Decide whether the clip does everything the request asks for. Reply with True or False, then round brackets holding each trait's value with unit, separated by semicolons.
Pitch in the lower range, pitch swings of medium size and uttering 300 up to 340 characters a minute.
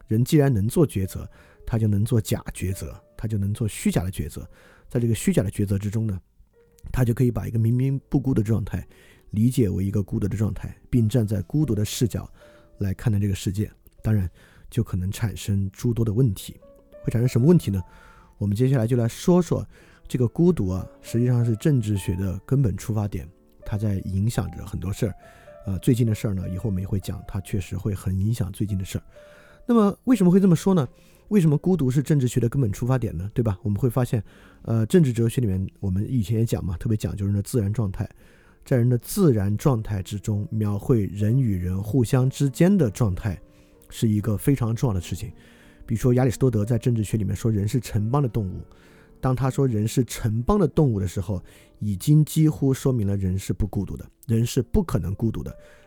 True (110 Hz; 4.5 semitones; 320 characters per minute)